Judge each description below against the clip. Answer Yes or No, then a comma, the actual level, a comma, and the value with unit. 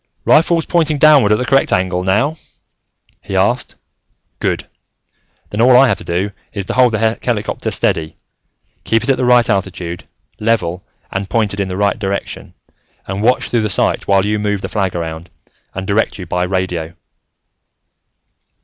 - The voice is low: Yes, low, 105 Hz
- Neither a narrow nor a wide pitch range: Yes, average, 4.4 semitones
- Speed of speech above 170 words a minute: No, average, 165 wpm